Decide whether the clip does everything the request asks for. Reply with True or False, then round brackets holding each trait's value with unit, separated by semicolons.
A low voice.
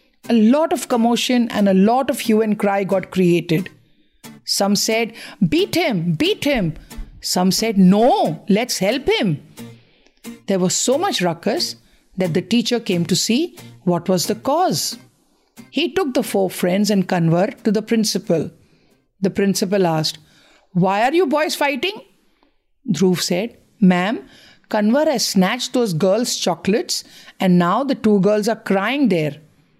False (205 Hz)